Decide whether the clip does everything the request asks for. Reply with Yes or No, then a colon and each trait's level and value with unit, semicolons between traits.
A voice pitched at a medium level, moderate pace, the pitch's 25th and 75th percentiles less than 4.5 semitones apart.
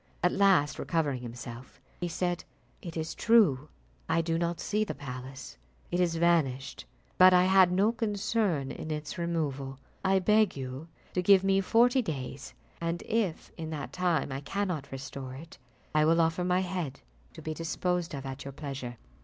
No: medium, 165 Hz; average, 170 wpm; average, 4.9 semitones